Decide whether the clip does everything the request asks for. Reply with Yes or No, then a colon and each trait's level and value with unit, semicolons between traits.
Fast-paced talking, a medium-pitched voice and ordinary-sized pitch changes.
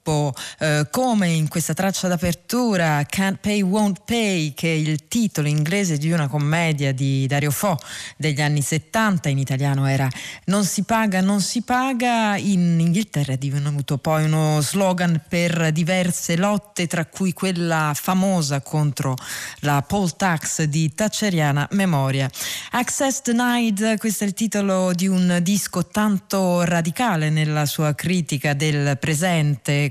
No: average, 140 wpm; medium, 170 Hz; average, 4.9 semitones